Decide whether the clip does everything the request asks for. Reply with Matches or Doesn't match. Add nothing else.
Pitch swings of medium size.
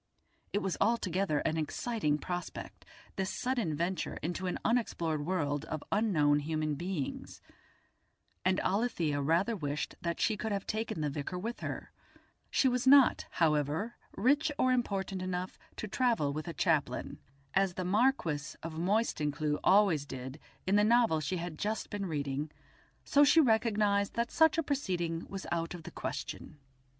Doesn't match